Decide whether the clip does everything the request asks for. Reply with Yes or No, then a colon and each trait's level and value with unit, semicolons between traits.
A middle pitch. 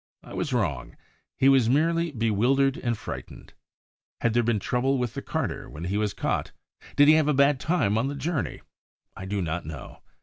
No: low, 125 Hz